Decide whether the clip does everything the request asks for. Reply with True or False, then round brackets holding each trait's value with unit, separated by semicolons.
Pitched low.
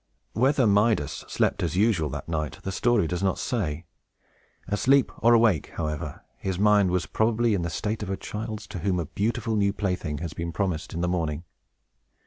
True (95 Hz)